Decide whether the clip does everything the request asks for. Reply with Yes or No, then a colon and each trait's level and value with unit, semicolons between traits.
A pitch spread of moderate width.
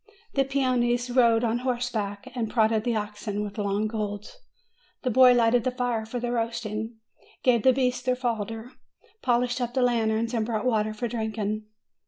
No: narrow, 2.3 semitones